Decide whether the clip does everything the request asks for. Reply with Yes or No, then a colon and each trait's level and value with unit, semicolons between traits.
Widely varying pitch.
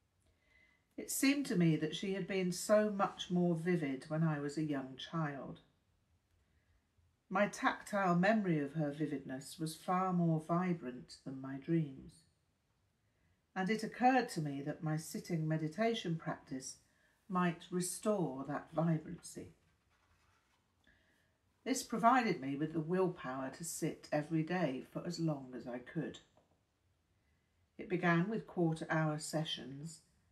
Yes: wide, 6.4 semitones